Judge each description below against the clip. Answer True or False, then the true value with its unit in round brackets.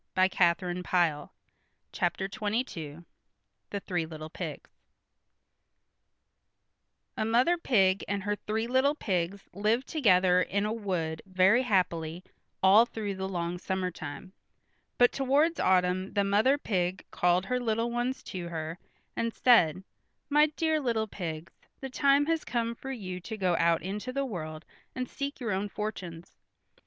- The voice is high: True (195 Hz)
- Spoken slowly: False (145 wpm)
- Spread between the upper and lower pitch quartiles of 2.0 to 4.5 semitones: False (5.1 semitones)